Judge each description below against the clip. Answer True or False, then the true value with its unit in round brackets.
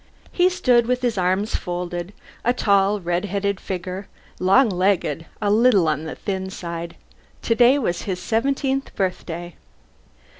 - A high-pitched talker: True (195 Hz)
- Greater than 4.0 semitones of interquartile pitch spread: True (4.7 semitones)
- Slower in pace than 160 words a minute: True (140 wpm)